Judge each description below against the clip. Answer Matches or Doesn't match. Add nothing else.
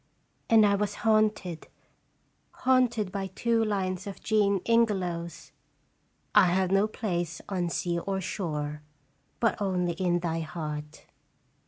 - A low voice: Doesn't match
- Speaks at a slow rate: Matches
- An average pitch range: Matches